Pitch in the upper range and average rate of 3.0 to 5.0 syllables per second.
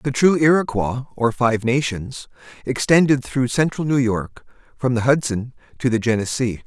No: low, 125 Hz; 4.7 syllables/s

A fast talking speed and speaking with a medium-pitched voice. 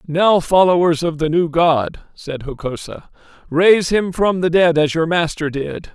No: average, 170 wpm; medium, 165 Hz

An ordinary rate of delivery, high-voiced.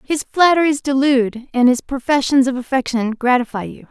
Yes: average, 155 wpm; very high, 260 Hz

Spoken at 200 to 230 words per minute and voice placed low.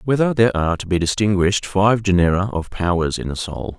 Yes: fast, 205 wpm; very low, 95 Hz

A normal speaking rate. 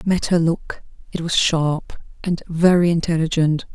Yes: average, 160 wpm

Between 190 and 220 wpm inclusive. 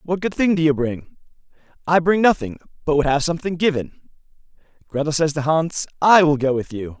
Yes: average, 195 wpm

